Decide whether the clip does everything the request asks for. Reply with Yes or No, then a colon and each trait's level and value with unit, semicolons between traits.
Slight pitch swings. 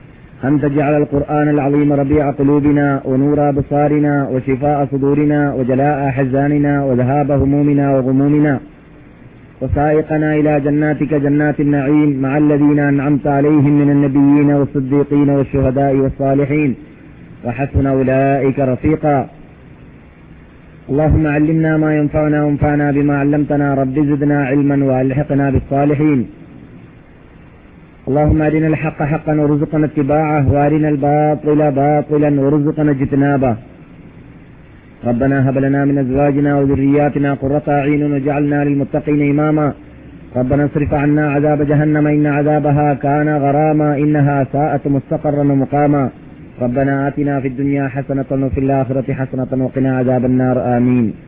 Yes: narrow, 1.3 semitones